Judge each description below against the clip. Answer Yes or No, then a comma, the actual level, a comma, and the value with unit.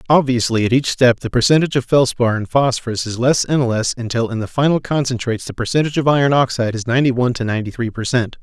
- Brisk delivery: Yes, fast, 230 wpm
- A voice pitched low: Yes, low, 125 Hz